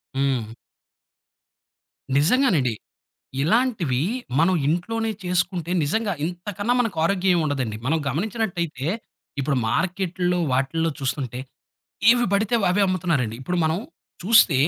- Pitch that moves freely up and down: Yes, wide, 6.2 semitones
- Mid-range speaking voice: Yes, medium, 175 Hz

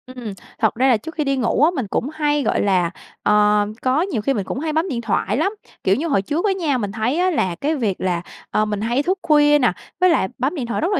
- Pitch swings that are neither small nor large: No, wide, 6.7 semitones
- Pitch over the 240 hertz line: Yes, very high, 260 Hz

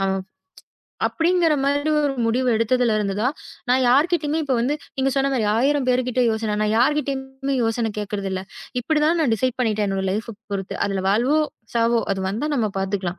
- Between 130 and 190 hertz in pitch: No, very high, 250 Hz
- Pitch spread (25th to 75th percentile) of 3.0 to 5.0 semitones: Yes, average, 4.5 semitones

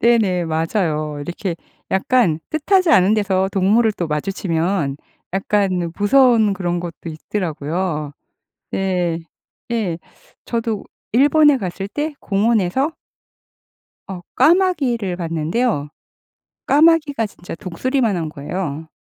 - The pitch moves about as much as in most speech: No, wide, 5.8 semitones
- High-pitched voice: Yes, high, 195 Hz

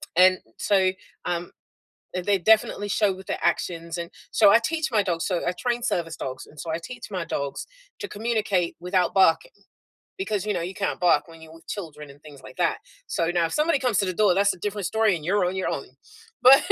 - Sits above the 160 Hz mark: Yes, medium, 185 Hz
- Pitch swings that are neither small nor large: Yes, average, 3.7 semitones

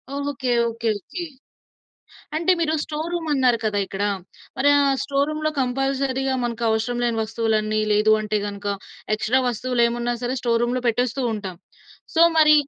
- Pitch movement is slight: No, average, 3.8 semitones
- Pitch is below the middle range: No, high, 245 Hz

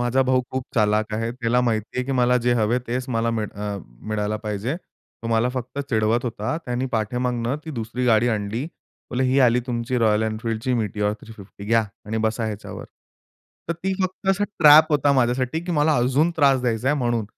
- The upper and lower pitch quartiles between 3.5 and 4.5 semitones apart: No, average, 2.9 semitones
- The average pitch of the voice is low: Yes, low, 120 Hz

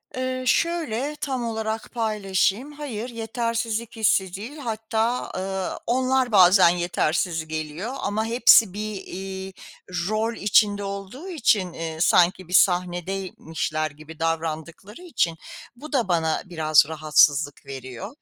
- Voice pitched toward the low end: No, high, 200 Hz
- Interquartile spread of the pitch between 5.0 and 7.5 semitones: Yes, wide, 5.4 semitones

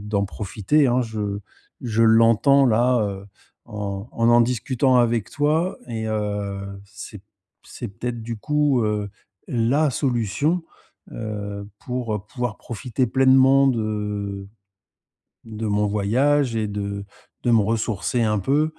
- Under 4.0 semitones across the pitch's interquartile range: Yes, average, 3.5 semitones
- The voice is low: Yes, low, 115 Hz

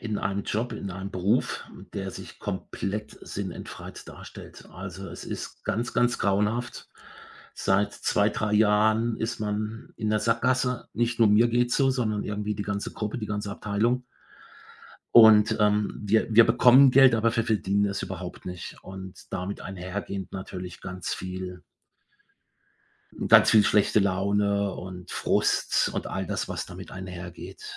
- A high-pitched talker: No, low, 105 Hz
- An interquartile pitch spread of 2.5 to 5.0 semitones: Yes, average, 2.8 semitones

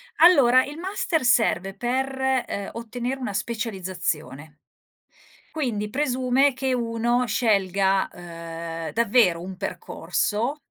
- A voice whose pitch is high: Yes, high, 230 Hz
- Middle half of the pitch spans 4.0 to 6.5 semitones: Yes, average, 5.3 semitones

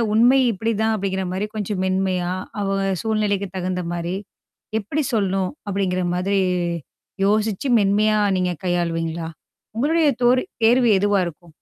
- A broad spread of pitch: No, average, 3.0 semitones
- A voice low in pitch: No, high, 195 Hz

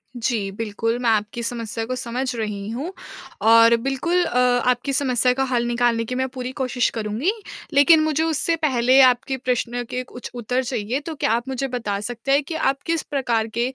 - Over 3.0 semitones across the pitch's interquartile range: No, narrow, 2.6 semitones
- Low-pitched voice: No, very high, 250 Hz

